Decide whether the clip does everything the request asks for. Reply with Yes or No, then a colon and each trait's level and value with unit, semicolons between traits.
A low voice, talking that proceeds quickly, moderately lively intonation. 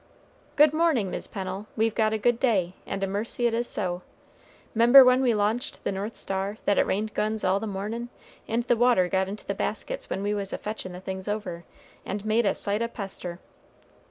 No: high, 210 Hz; fast, 215 wpm; average, 3.3 semitones